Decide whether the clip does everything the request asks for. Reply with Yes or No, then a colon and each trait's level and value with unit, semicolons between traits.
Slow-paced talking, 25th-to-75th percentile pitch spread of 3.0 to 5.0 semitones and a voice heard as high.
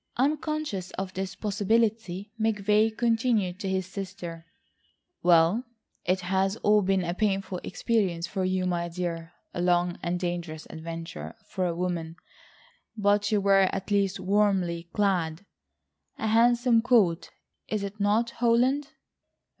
Yes: slow, 130 wpm; average, 3.4 semitones; high, 195 Hz